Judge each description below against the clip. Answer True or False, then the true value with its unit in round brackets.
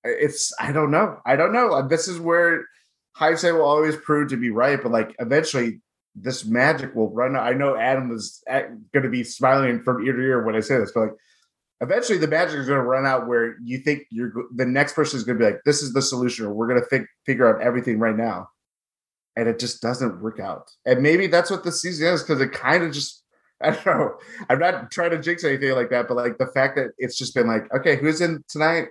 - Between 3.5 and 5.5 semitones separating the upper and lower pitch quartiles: True (4.2 semitones)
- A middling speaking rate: False (245 wpm)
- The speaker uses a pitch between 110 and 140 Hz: True (135 Hz)